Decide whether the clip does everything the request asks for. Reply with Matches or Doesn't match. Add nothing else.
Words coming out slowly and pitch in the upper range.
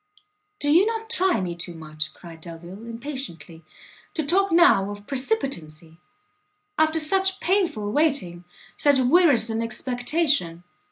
Matches